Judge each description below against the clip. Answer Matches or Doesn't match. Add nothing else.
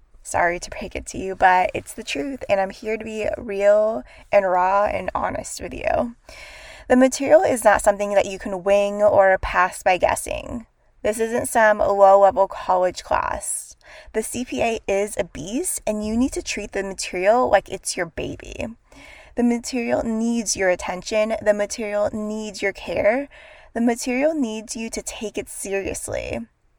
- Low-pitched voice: Doesn't match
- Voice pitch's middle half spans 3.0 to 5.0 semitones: Matches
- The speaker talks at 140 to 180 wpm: Matches